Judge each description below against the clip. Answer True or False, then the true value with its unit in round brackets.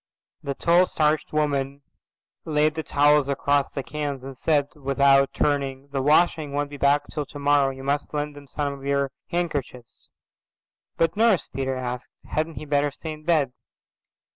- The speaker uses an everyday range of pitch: False (1.6 semitones)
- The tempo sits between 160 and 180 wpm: True (165 wpm)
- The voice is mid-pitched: True (145 Hz)